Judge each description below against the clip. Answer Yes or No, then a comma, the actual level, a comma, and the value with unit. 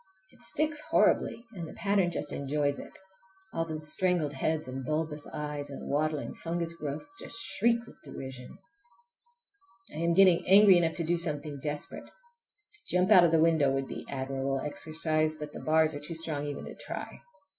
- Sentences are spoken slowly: No, average, 175 wpm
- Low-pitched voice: No, medium, 155 Hz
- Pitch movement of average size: Yes, average, 3.1 semitones